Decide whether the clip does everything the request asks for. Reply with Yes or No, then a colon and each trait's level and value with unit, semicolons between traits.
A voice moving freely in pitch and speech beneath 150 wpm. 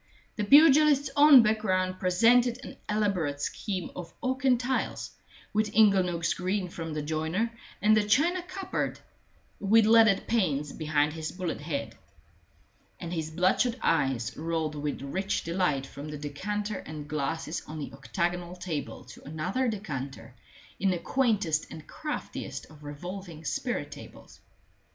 Yes: wide, 6.0 semitones; average, 140 wpm